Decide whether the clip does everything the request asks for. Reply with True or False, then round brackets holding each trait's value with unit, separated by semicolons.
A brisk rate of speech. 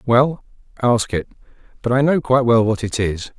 False (195 wpm)